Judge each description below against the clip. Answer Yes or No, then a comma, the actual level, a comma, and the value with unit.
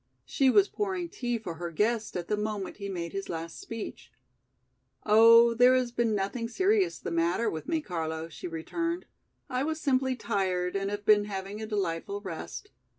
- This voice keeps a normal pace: Yes, average, 180 wpm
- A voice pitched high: Yes, high, 210 Hz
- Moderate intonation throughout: No, wide, 5.8 semitones